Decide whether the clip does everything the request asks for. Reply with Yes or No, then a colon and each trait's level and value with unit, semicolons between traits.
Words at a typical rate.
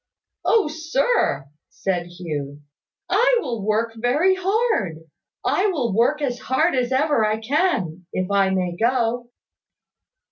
No: slow, 130 wpm